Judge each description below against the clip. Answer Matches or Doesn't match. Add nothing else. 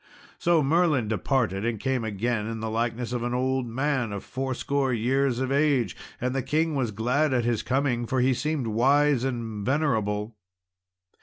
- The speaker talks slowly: Doesn't match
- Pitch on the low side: Matches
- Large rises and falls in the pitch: Doesn't match